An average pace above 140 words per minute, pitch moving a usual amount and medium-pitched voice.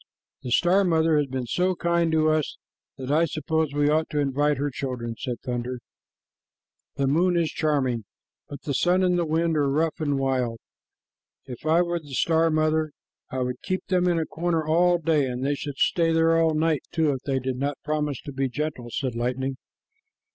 Yes: average, 200 wpm; average, 3.5 semitones; medium, 150 Hz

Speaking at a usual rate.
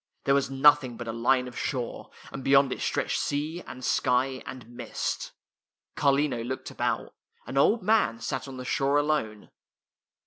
Yes: average, 165 wpm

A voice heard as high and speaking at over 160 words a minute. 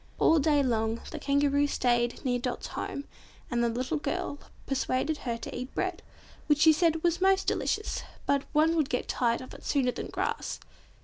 Yes: very high, 280 Hz; average, 185 wpm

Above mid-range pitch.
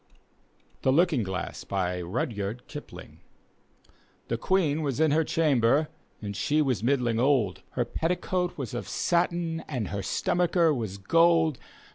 No: medium, 140 Hz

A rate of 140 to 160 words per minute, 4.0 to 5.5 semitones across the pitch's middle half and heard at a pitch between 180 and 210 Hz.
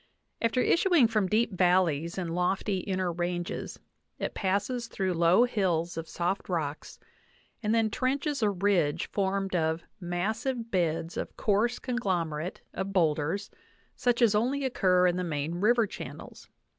Yes: average, 145 wpm; average, 4.5 semitones; high, 190 Hz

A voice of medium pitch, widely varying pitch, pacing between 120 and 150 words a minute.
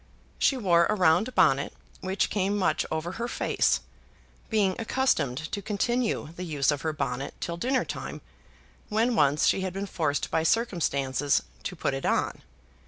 No: medium, 180 Hz; wide, 5.8 semitones; average, 165 wpm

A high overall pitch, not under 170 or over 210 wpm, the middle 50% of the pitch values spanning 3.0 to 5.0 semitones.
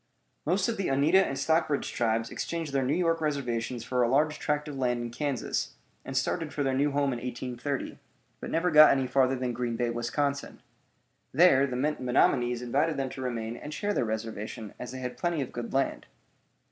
No: low, 135 Hz; average, 195 wpm; average, 3.6 semitones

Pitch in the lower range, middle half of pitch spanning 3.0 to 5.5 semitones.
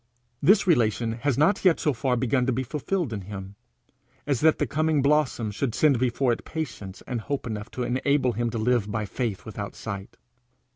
Yes: low, 125 Hz; average, 4.7 semitones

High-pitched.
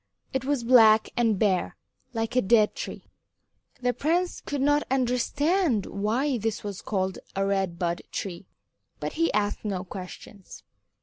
Yes: high, 225 Hz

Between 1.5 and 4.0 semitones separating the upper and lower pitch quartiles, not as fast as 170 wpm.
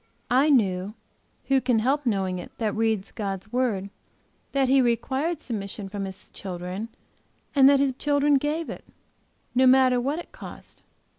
No: wide, 5.5 semitones; average, 155 wpm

